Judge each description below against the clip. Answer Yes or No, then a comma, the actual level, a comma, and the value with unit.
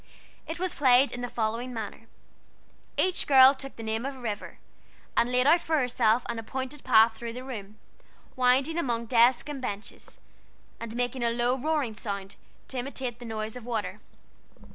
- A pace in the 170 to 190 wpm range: Yes, average, 180 wpm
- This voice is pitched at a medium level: No, high, 245 Hz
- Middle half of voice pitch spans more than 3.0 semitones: No, average, 2.7 semitones